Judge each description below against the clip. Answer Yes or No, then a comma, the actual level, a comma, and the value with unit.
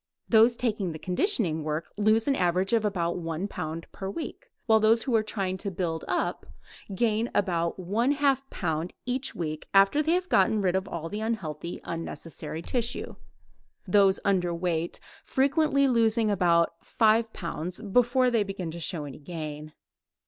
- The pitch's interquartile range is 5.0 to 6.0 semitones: Yes, average, 5.3 semitones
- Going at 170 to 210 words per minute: No, average, 155 wpm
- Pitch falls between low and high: No, high, 195 Hz